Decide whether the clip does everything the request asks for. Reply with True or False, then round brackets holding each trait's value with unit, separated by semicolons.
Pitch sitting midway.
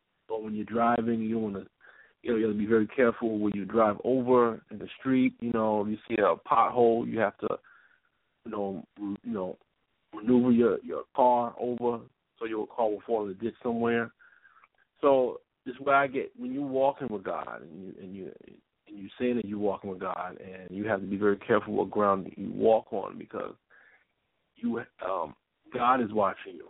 False (115 Hz)